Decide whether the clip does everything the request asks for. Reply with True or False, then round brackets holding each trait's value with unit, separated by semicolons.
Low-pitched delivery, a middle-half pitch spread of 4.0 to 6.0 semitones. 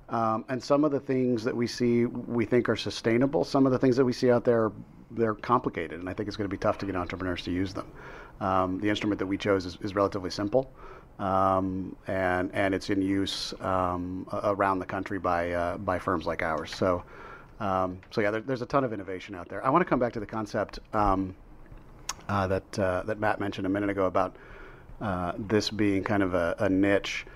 False (100 Hz; 3.4 semitones)